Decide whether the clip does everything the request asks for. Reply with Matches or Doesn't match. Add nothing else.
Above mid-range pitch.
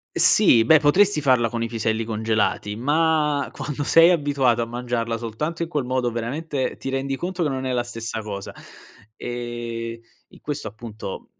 Doesn't match